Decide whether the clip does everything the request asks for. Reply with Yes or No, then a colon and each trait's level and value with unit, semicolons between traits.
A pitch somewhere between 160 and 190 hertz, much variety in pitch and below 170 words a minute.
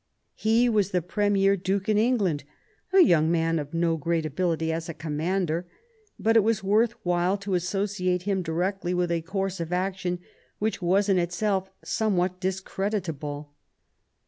No: medium, 185 Hz; average, 3.0 semitones; average, 155 wpm